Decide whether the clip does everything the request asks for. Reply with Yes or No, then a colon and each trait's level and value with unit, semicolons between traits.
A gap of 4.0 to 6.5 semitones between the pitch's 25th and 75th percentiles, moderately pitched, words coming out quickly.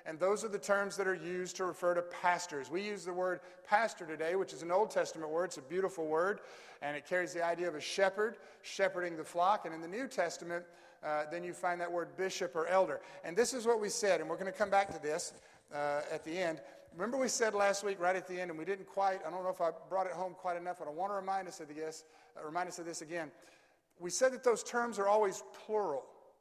No: average, 2.9 semitones; medium, 180 Hz; fast, 265 wpm